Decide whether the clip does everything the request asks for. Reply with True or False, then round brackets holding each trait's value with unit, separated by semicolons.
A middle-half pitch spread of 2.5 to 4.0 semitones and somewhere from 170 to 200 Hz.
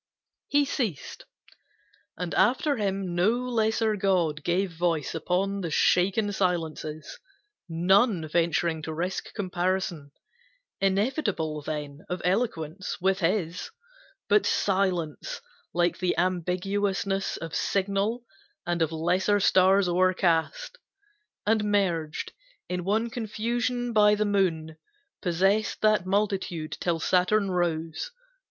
True (3.4 semitones; 185 Hz)